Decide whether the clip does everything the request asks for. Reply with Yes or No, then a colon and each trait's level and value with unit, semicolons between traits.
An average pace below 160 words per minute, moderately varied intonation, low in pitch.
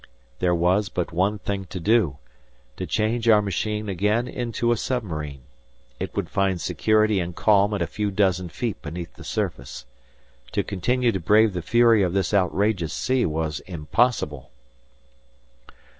Yes: average, 150 wpm; average, 3.8 semitones; low, 100 Hz